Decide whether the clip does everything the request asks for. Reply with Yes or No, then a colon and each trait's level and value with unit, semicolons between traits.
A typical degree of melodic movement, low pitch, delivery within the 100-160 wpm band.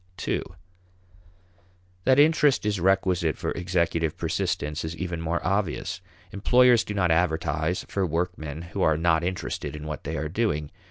Yes: average, 3.4 semitones; very low, 85 Hz; average, 150 wpm